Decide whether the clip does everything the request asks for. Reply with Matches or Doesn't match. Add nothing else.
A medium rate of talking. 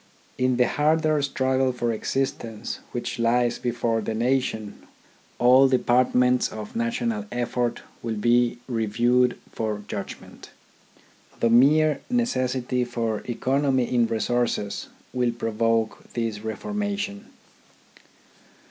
Doesn't match